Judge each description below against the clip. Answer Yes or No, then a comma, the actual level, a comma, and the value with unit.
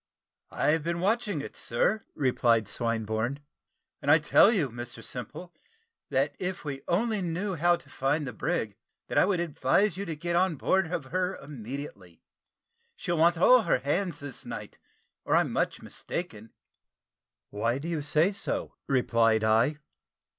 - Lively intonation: Yes, wide, 6.5 semitones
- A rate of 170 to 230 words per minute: No, average, 155 wpm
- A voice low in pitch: No, medium, 150 Hz